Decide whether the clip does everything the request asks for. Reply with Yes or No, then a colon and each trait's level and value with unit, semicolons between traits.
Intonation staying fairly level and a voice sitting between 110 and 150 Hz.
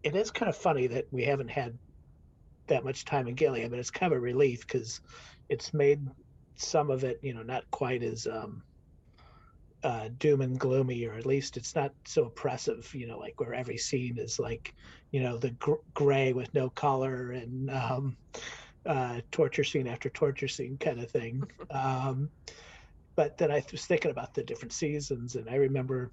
Yes: narrow, 2.3 semitones; low, 130 Hz